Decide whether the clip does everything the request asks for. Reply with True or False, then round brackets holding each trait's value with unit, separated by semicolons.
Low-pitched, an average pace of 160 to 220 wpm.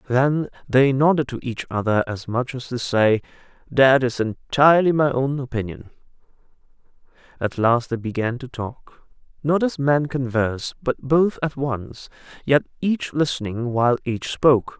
False (130 Hz; 150 wpm)